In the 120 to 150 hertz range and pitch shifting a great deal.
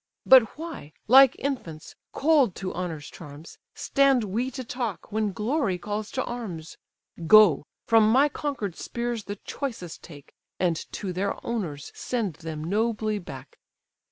No: high, 215 Hz; wide, 5.9 semitones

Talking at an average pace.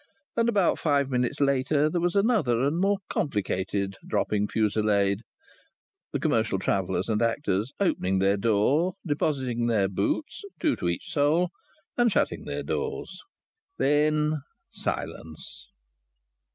No: slow, 125 wpm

